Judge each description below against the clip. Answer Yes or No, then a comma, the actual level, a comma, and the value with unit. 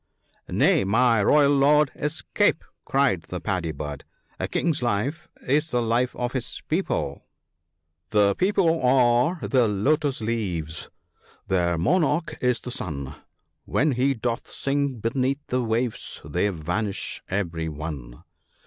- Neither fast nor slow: Yes, average, 145 wpm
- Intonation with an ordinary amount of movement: No, wide, 7.9 semitones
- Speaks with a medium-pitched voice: No, low, 120 Hz